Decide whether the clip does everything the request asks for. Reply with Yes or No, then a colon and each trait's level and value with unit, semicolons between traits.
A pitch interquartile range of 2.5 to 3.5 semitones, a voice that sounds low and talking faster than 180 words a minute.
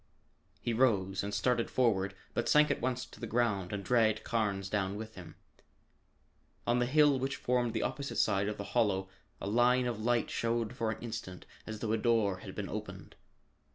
Yes: average, 3.2 semitones; low, 115 Hz; average, 190 wpm